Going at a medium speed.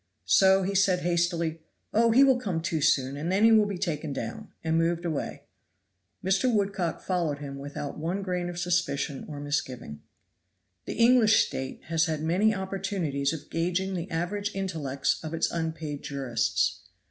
Yes: average, 165 wpm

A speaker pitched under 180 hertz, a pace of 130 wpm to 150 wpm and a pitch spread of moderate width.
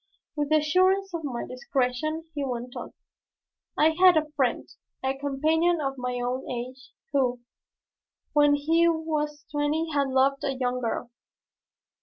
No: very high, 285 Hz; average, 145 wpm; average, 3.6 semitones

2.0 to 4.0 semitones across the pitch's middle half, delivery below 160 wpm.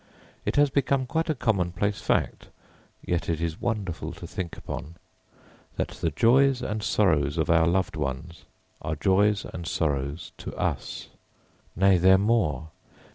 No: wide, 5.4 semitones; average, 150 wpm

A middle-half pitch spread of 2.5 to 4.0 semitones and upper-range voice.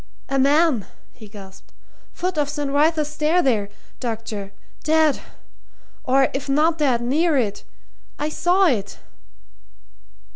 No: average, 5.0 semitones; very high, 285 Hz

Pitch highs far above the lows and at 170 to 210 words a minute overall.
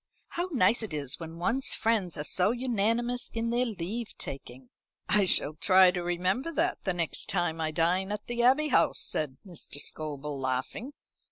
Yes: wide, 6.8 semitones; average, 175 wpm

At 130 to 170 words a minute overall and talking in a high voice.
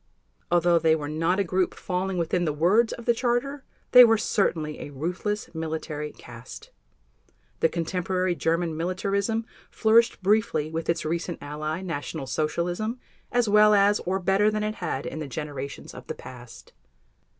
No: average, 160 wpm; medium, 175 Hz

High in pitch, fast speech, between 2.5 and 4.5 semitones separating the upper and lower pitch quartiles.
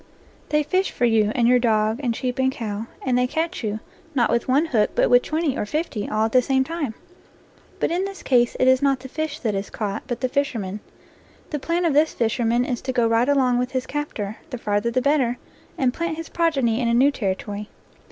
Yes: very high, 250 Hz; fast, 230 wpm; average, 4.0 semitones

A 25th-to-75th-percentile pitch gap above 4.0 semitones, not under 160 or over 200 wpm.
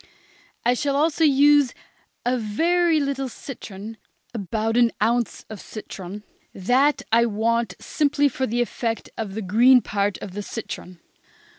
No: average, 4.6 semitones; average, 140 wpm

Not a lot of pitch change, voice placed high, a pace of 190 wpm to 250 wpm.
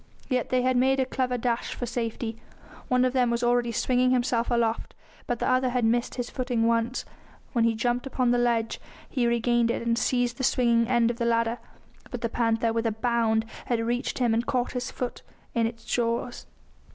Yes: narrow, 1.3 semitones; high, 240 Hz; fast, 205 wpm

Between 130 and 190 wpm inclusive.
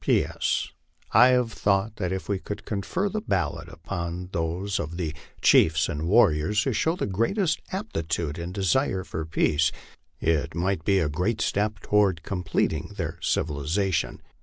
Yes: average, 160 wpm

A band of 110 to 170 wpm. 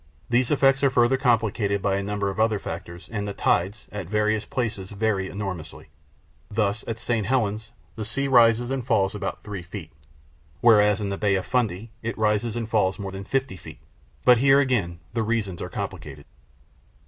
No: average, 185 wpm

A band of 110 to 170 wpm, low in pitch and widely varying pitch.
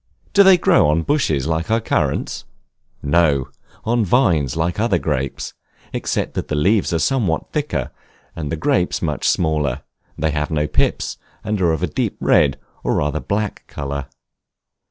Yes: average, 160 wpm; very low, 80 Hz; wide, 6.3 semitones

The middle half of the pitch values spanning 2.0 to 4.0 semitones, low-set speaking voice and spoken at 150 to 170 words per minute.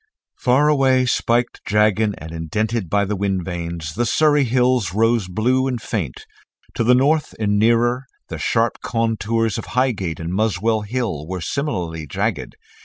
No: average, 5.0 semitones; low, 110 Hz; average, 155 wpm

